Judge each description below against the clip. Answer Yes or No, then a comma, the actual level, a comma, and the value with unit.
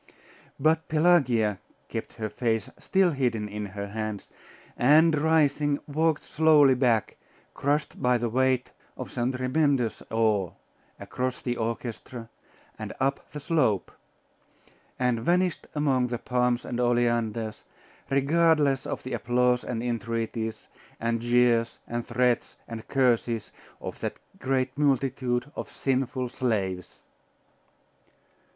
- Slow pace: Yes, slow, 120 wpm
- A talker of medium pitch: No, low, 125 Hz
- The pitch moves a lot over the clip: No, average, 3.3 semitones